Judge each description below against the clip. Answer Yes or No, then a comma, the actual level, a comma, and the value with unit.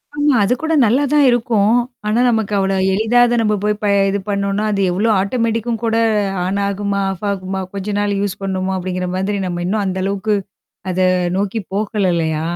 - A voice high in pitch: Yes, high, 200 Hz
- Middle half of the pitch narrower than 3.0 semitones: Yes, narrow, 2.6 semitones